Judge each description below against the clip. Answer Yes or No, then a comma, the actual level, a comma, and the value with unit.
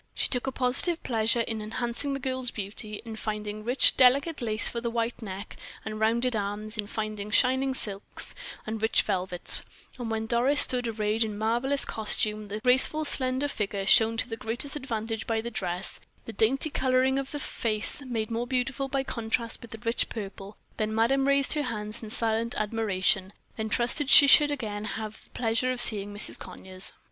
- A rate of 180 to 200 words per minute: Yes, average, 185 wpm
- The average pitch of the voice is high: Yes, high, 230 Hz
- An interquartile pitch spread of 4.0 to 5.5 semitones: No, average, 3.1 semitones